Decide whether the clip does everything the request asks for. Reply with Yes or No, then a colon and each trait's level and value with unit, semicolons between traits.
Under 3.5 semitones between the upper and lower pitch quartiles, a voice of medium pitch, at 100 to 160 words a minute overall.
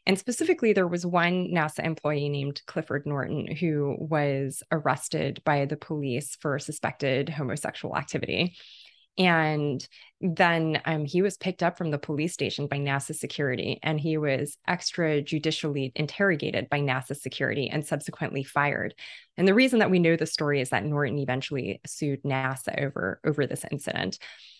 Yes: average, 2.8 semitones; medium, 150 Hz; average, 155 wpm